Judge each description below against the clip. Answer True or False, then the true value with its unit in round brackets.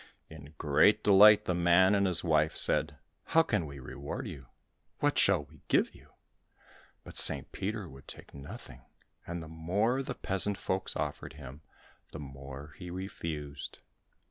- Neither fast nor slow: True (155 wpm)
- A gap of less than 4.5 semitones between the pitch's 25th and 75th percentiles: False (5.1 semitones)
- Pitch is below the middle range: True (80 Hz)